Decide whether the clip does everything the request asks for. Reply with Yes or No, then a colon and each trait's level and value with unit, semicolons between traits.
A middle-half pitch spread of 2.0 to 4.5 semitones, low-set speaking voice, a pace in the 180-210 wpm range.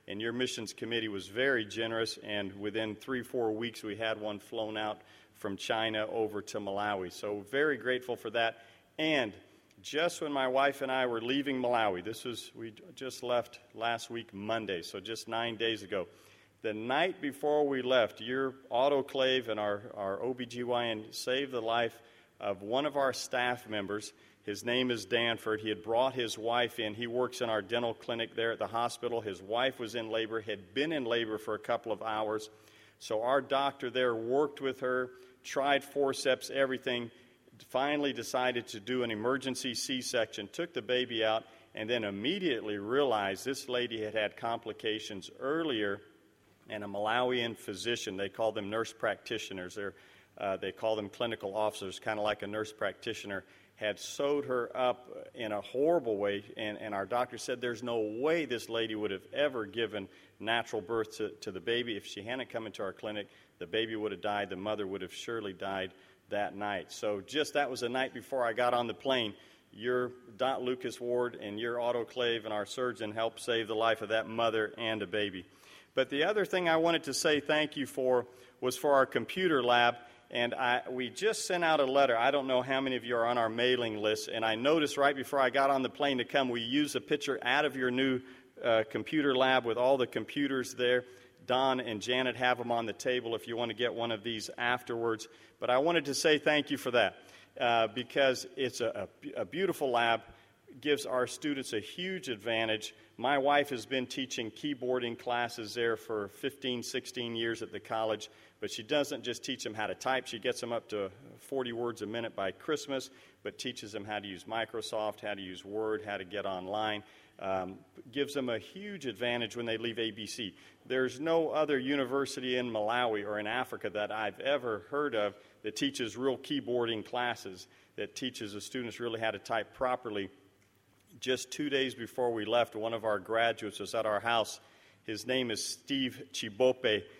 Yes: average, 3.1 semitones; low, 120 Hz; average, 195 wpm